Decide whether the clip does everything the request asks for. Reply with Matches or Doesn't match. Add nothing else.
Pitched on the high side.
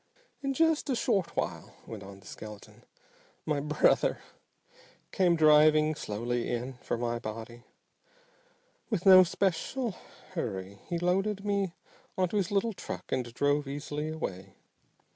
Doesn't match